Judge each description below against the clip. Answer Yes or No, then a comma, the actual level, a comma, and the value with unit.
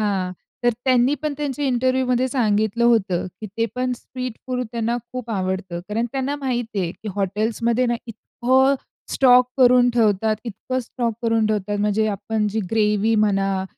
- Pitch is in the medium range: No, high, 230 Hz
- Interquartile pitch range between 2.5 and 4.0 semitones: Yes, average, 3.2 semitones